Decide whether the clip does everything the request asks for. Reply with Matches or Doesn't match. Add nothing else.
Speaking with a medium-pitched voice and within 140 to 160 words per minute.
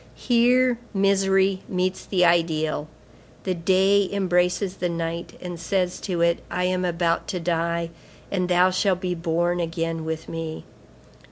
Matches